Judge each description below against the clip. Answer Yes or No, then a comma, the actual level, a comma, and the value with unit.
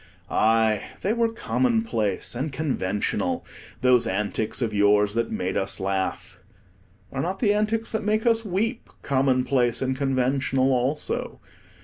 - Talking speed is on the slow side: Yes, slow, 130 wpm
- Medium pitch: No, low, 130 Hz